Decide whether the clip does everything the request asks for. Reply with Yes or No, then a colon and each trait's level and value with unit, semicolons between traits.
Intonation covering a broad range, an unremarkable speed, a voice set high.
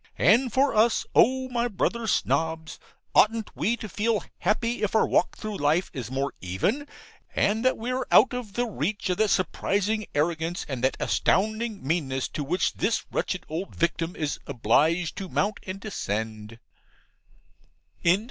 Yes: wide, 6.2 semitones; average, 155 wpm; high, 195 Hz